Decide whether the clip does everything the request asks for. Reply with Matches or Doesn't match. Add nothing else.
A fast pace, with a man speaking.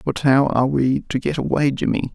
Matches